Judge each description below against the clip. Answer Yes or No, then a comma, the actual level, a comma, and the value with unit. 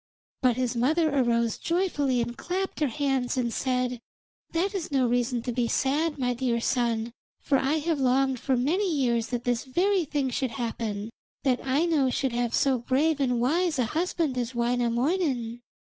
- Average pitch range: Yes, average, 3.7 semitones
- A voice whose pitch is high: Yes, very high, 260 Hz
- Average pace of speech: Yes, average, 175 wpm